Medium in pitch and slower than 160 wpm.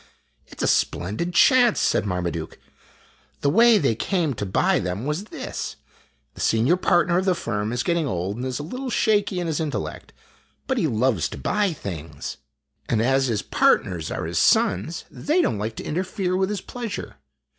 No: medium, 150 Hz; average, 190 wpm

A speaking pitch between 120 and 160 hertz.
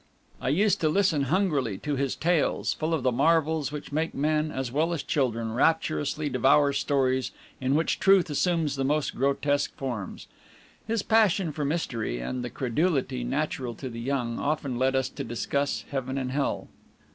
Yes: medium, 140 Hz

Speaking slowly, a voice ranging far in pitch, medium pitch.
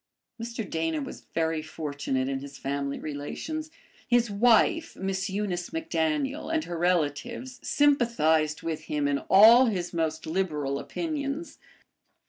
Yes: slow, 125 wpm; wide, 7.7 semitones; medium, 175 Hz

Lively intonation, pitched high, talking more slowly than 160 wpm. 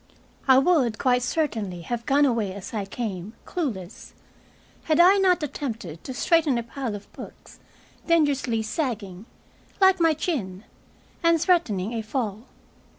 Yes: wide, 6.9 semitones; high, 245 Hz; average, 140 wpm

